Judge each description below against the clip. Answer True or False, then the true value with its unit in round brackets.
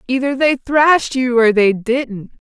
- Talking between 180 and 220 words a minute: False (165 wpm)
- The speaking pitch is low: False (250 Hz)